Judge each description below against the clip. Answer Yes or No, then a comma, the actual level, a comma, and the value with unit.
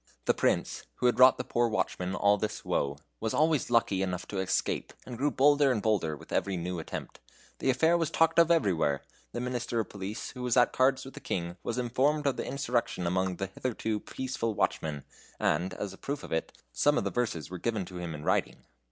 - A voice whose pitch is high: No, low, 115 Hz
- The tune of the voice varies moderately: No, wide, 6.0 semitones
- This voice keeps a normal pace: No, fast, 220 wpm